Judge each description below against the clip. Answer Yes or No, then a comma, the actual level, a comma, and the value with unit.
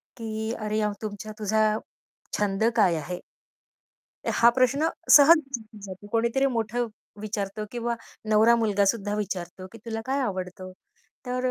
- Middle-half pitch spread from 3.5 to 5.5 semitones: No, narrow, 2.6 semitones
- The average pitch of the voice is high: Yes, high, 220 Hz